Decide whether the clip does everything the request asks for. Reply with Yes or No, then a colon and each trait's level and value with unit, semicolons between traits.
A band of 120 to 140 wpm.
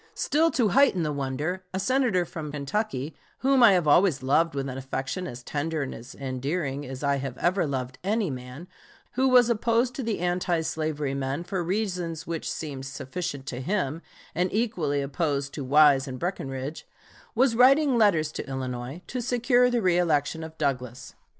No: average, 170 wpm